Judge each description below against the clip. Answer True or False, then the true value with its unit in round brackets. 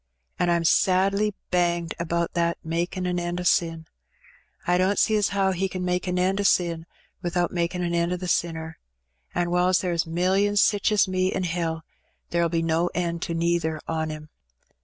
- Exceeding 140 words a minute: True (195 wpm)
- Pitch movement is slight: True (1.5 semitones)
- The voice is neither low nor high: True (175 Hz)